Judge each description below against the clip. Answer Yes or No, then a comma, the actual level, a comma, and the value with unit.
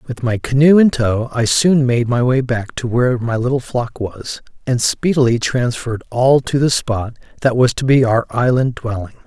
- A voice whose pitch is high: No, low, 125 Hz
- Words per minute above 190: Yes, average, 200 wpm